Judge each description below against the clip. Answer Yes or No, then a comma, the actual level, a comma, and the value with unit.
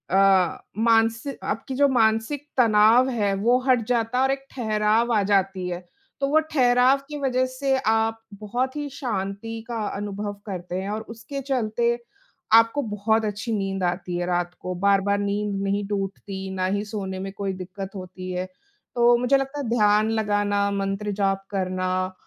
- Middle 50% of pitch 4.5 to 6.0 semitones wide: No, average, 3.5 semitones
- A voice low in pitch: No, high, 210 Hz